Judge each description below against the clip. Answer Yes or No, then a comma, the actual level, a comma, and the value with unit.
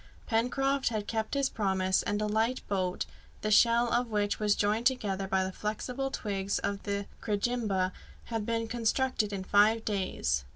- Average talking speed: Yes, average, 165 wpm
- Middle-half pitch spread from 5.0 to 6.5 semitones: No, average, 2.8 semitones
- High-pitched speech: Yes, high, 215 Hz